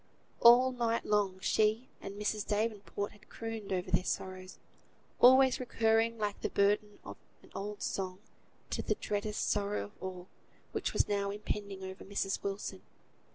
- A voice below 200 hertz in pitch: No, high, 205 Hz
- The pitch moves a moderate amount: No, narrow, 2.2 semitones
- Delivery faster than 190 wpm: No, average, 155 wpm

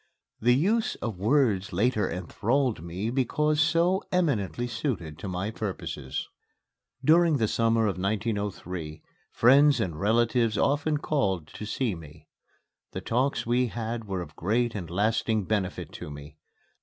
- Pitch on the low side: Yes, low, 110 Hz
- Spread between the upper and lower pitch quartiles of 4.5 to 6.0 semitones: Yes, wide, 5.5 semitones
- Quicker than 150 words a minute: No, average, 140 wpm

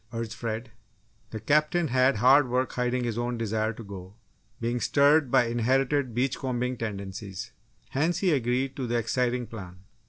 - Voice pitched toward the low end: Yes, low, 120 Hz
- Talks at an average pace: Yes, average, 160 wpm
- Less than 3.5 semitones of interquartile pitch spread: Yes, average, 2.8 semitones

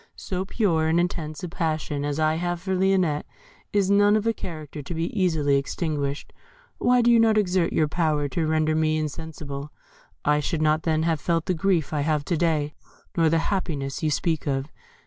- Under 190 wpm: No, average, 195 wpm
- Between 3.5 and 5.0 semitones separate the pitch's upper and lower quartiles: No, average, 3.0 semitones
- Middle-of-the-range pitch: Yes, medium, 160 Hz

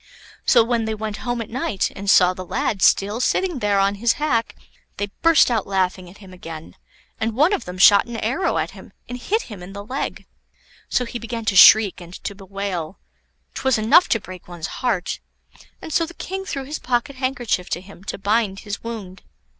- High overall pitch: Yes, high, 215 Hz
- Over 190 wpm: Yes, fast, 205 wpm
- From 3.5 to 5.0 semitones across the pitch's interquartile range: Yes, average, 4.2 semitones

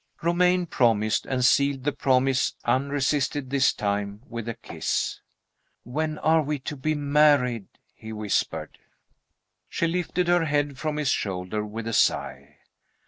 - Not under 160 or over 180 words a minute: No, average, 140 wpm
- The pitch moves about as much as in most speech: Yes, average, 4.8 semitones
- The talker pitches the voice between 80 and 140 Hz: Yes, low, 135 Hz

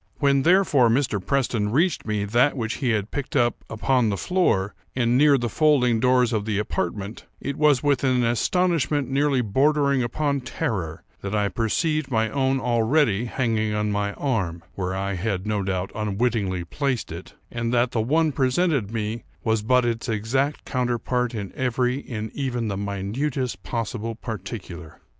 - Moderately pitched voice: No, low, 120 Hz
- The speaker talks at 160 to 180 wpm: Yes, average, 165 wpm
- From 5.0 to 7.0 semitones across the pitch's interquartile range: No, average, 4.2 semitones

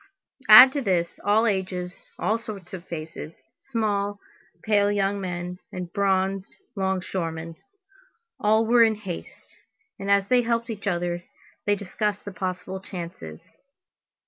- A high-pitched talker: Yes, high, 195 Hz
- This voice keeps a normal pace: No, slow, 130 wpm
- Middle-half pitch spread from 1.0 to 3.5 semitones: Yes, average, 2.8 semitones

